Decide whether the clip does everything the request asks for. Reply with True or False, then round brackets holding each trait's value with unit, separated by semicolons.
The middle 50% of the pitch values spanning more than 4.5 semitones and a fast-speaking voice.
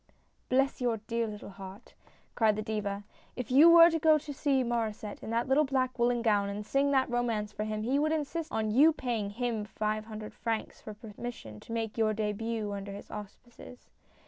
False (3.5 semitones; 220 wpm)